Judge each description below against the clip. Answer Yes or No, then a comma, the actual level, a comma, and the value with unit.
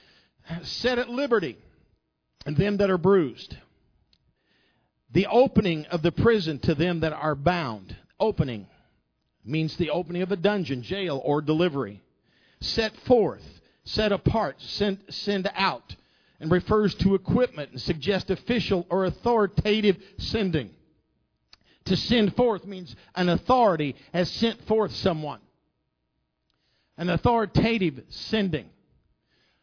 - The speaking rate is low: Yes, slow, 115 wpm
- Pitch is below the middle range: No, medium, 180 Hz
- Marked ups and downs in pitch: No, average, 5.0 semitones